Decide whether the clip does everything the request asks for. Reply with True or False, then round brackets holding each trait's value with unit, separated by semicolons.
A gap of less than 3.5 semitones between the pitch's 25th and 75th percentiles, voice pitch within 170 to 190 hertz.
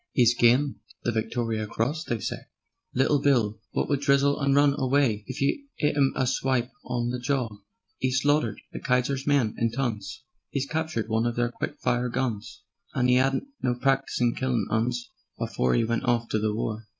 False (2.9 semitones; 125 Hz)